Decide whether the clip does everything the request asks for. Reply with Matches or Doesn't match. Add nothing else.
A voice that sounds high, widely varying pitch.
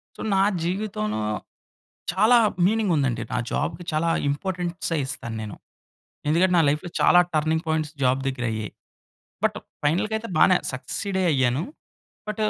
Doesn't match